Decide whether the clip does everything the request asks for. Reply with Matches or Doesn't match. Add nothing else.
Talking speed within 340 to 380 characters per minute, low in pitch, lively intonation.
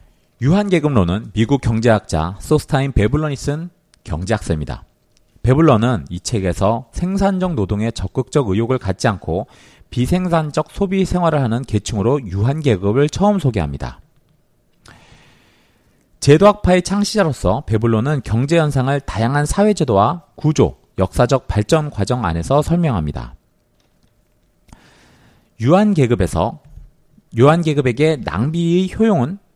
Doesn't match